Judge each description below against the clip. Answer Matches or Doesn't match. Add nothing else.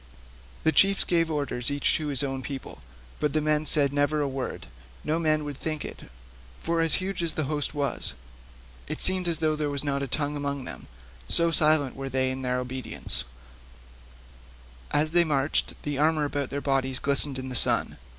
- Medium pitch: Matches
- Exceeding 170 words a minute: Matches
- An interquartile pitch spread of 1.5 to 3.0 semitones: Matches